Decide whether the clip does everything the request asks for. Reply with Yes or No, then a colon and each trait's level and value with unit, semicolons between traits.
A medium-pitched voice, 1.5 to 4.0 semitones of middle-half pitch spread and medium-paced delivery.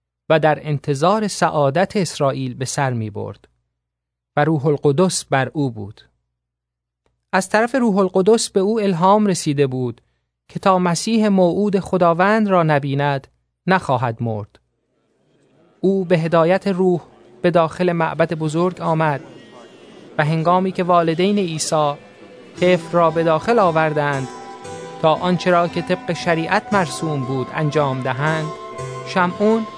No: medium, 160 Hz; wide, 5.5 semitones; average, 125 wpm